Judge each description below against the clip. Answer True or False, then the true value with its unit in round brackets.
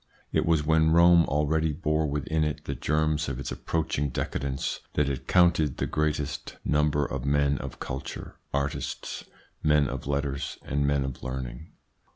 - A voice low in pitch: True (75 Hz)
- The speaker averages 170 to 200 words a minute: False (160 wpm)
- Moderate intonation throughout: False (2.0 semitones)